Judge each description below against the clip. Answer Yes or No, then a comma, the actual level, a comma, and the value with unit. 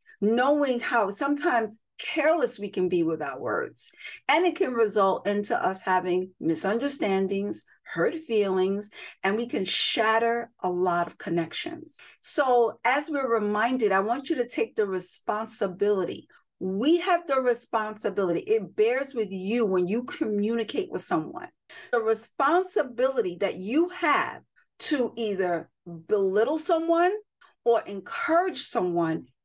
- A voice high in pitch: Yes, high, 230 Hz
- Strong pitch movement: Yes, wide, 8.4 semitones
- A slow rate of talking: Yes, slow, 130 wpm